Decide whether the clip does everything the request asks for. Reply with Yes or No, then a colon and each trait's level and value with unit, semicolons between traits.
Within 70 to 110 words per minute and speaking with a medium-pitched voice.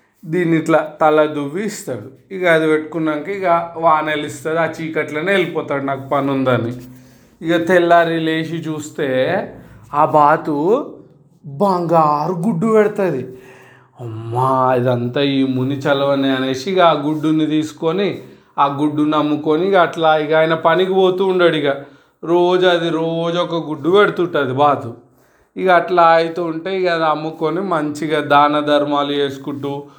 No: average, 120 wpm; medium, 155 Hz